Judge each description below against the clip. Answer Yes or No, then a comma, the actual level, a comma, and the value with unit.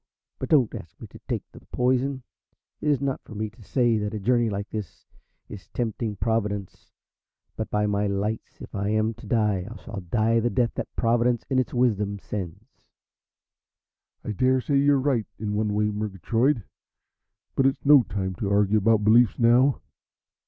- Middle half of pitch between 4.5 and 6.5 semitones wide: No, average, 3.1 semitones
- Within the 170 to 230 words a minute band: Yes, average, 175 wpm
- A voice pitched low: Yes, low, 110 Hz